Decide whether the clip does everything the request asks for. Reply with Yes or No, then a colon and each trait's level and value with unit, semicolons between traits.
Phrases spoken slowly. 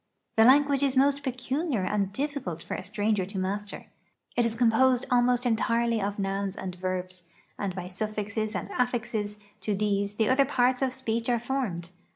No: average, 175 wpm